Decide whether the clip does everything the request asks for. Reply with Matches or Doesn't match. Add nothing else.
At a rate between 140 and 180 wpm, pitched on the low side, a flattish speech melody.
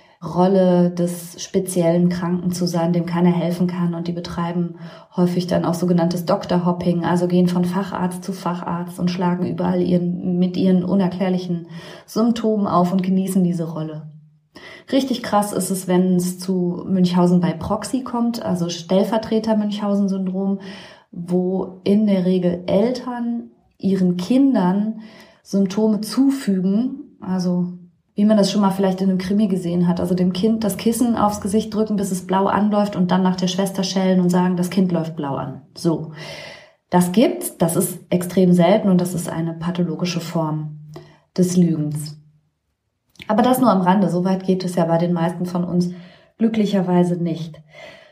Doesn't match